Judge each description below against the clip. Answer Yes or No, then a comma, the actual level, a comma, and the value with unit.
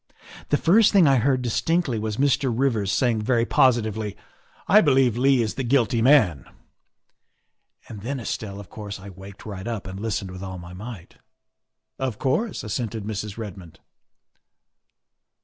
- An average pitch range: Yes, average, 4.8 semitones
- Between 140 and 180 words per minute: Yes, average, 170 wpm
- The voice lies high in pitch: No, low, 115 Hz